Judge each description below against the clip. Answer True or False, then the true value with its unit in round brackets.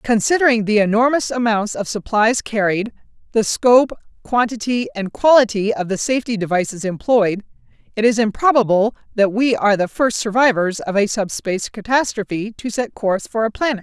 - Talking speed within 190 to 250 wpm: False (155 wpm)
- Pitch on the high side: True (220 Hz)